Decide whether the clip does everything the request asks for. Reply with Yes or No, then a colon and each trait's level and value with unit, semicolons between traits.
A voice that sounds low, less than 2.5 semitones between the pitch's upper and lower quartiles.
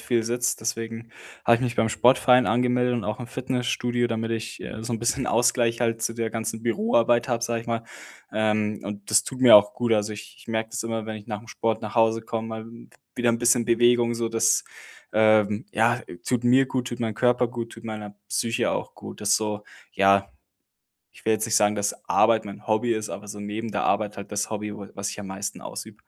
Yes: low, 115 Hz; narrow, 1.9 semitones